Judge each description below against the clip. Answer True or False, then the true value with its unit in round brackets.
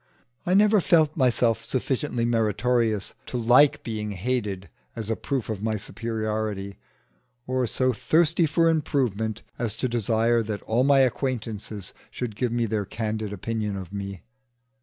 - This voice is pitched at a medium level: False (115 Hz)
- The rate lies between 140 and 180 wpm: True (145 wpm)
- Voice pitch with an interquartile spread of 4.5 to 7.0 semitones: False (3.2 semitones)